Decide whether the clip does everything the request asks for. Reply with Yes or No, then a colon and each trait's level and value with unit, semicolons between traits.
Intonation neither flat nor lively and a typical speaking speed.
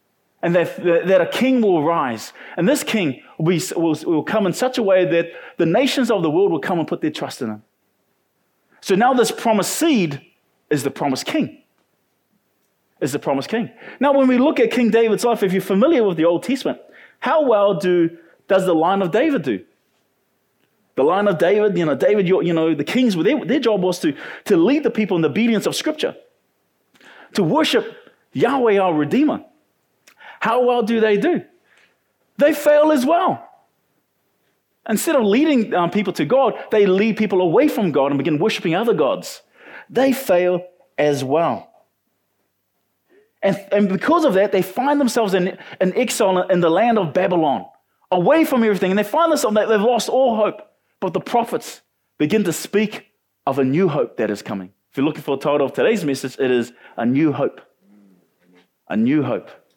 No: wide, 6.5 semitones; average, 190 wpm